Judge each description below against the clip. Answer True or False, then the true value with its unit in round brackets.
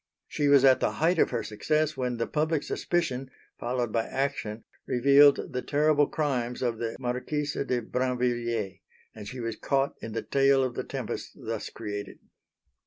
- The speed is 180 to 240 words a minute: False (170 wpm)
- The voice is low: True (125 Hz)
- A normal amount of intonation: True (3.4 semitones)